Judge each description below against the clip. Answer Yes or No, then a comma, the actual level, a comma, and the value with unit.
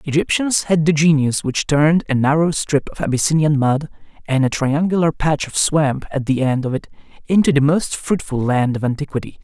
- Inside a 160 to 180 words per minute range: No, average, 190 wpm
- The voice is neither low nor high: Yes, medium, 150 Hz